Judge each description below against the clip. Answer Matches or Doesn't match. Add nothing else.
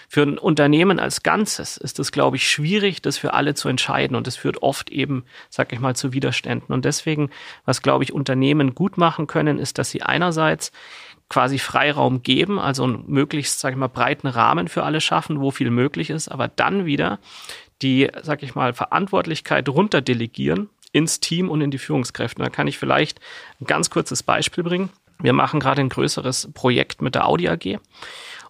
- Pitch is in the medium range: Matches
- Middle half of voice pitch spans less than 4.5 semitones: Matches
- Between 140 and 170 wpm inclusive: Doesn't match